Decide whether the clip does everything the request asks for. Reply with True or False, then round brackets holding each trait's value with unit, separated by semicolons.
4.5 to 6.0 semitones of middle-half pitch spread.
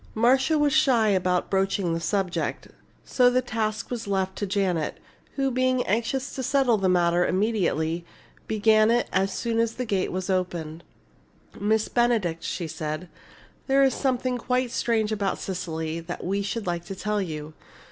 True (5.0 semitones)